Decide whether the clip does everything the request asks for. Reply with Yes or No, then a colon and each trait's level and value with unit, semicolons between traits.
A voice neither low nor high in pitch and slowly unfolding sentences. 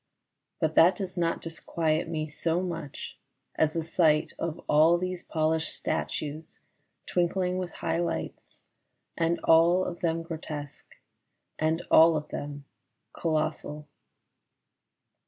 Yes: medium, 165 Hz; slow, 120 wpm